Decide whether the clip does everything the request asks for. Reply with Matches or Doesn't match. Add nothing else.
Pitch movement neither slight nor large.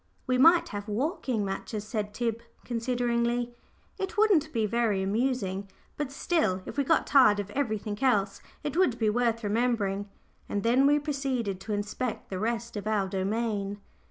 Matches